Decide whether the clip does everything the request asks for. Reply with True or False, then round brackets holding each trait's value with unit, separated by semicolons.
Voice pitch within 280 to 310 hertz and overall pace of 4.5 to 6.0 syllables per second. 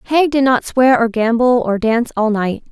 False (240 Hz; 4.7 syllables/s)